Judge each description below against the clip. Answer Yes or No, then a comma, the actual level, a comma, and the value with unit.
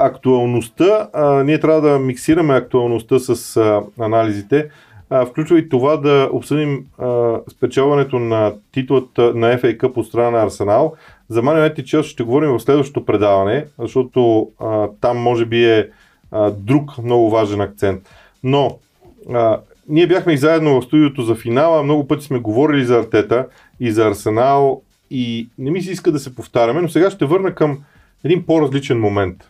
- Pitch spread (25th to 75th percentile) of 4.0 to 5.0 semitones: Yes, average, 4.6 semitones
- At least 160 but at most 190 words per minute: Yes, fast, 165 wpm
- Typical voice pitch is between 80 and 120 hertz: No, low, 130 Hz